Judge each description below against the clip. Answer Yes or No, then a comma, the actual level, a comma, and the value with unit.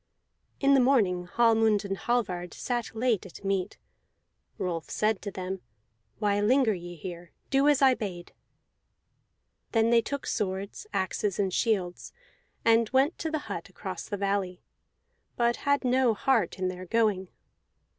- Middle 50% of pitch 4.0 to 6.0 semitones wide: Yes, average, 4.6 semitones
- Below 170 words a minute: Yes, average, 145 wpm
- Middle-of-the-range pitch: No, high, 210 Hz